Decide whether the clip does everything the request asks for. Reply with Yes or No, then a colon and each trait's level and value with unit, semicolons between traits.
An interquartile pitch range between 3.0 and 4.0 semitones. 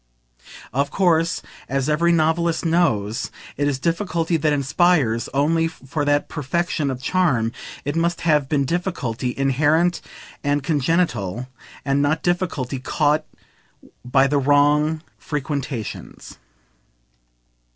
Yes: average, 3.5 semitones